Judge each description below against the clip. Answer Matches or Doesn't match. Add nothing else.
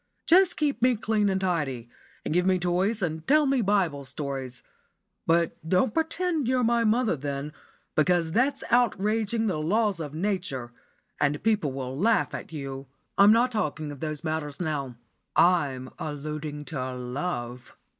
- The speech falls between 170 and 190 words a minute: Doesn't match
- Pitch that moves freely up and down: Matches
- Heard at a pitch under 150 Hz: Doesn't match